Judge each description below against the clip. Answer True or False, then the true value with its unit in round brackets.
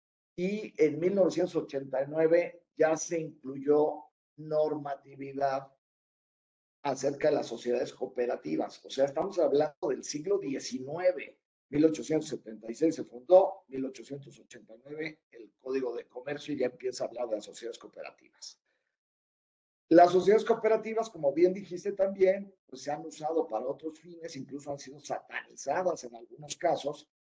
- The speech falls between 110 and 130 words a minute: True (125 wpm)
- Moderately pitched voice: True (155 Hz)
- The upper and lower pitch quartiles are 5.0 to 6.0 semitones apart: False (4.5 semitones)